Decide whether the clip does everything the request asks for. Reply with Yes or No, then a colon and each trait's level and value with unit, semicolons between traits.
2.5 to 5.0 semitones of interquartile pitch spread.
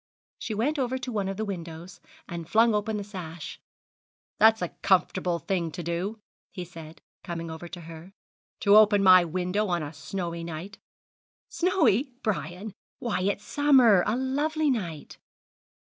Yes: average, 4.5 semitones